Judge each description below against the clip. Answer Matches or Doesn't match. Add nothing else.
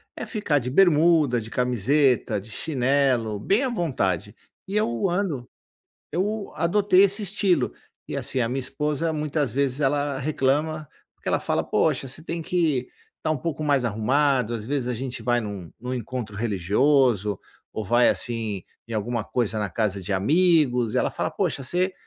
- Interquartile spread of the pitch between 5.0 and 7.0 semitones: Matches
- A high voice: Doesn't match